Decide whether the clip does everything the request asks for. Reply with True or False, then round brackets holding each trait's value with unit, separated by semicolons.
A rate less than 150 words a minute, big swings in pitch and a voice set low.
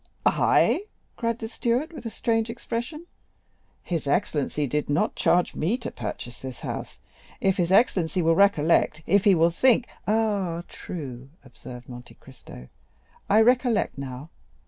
False (140 wpm; 7.7 semitones; 180 Hz)